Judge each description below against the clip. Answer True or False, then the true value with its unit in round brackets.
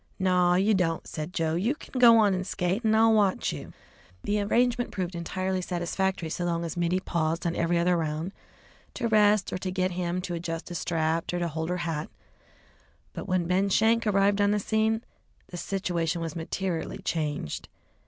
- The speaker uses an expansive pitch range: False (3.1 semitones)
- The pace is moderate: True (190 wpm)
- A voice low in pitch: False (180 Hz)